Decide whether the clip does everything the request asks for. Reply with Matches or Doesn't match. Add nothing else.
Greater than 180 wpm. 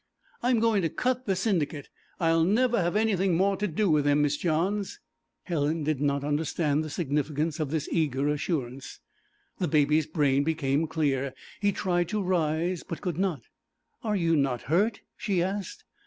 Doesn't match